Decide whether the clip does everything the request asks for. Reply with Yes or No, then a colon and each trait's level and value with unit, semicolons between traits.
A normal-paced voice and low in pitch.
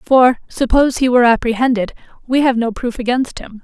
No: average, 180 wpm; high, 245 Hz